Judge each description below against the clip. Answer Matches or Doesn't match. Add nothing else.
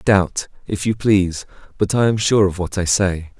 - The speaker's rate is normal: Doesn't match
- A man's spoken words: Matches